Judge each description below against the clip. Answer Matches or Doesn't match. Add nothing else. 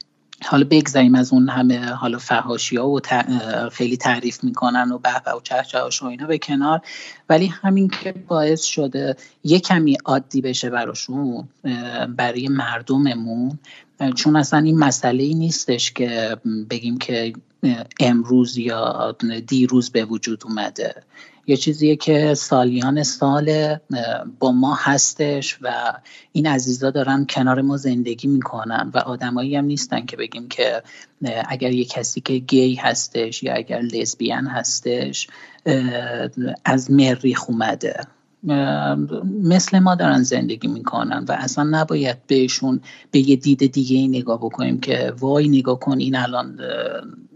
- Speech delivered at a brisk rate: Doesn't match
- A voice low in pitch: Matches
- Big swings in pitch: Doesn't match